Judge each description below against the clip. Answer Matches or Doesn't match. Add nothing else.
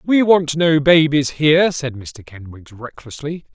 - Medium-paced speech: Matches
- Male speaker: Matches